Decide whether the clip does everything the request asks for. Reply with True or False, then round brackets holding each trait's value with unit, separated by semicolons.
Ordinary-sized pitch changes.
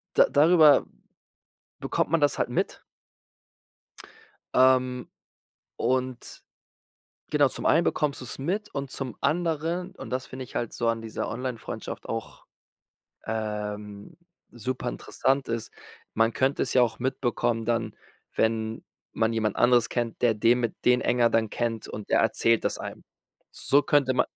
True (3.2 semitones)